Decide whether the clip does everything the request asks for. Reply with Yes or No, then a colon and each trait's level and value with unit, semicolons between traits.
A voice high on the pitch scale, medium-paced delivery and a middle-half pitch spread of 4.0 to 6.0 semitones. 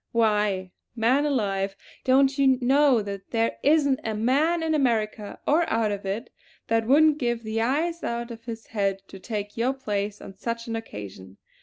Yes: high, 230 Hz; average, 175 wpm; average, 4.5 semitones